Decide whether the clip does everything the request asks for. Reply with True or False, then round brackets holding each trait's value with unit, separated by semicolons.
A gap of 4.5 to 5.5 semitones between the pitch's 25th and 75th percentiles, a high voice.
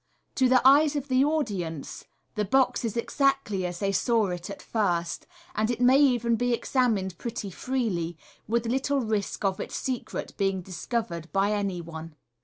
True (5.1 semitones; 220 Hz)